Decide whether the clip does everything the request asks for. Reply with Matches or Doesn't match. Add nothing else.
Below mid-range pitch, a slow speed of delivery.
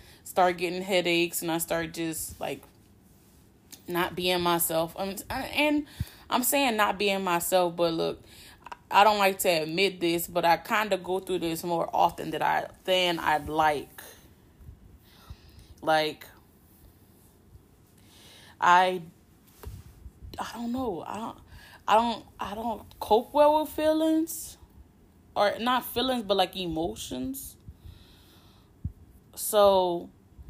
Doesn't match